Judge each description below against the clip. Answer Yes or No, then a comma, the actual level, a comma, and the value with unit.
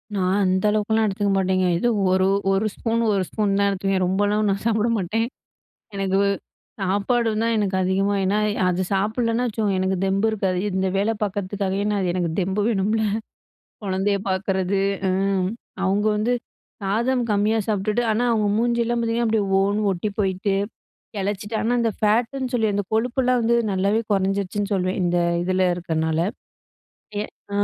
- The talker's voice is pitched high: Yes, high, 200 Hz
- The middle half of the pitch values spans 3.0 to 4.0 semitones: No, narrow, 2.5 semitones